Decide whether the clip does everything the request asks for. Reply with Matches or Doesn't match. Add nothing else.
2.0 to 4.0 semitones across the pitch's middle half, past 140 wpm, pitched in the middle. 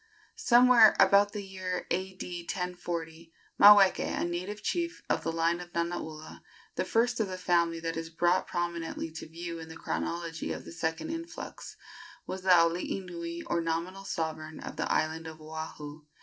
Matches